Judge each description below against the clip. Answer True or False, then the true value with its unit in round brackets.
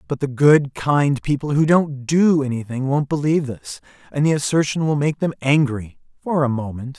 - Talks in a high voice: False (140 Hz)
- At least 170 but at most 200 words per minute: True (180 wpm)